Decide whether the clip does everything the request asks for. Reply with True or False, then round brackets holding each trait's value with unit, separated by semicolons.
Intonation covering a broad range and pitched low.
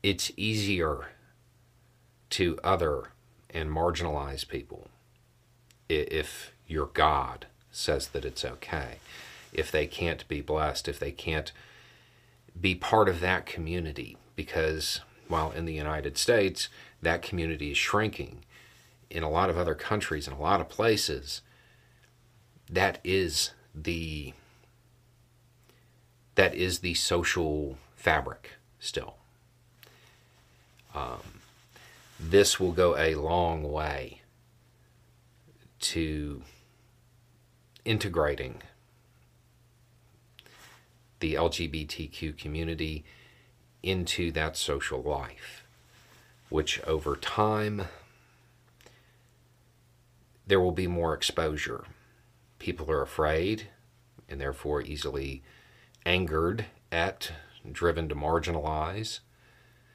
True (7.1 semitones; 100 Hz)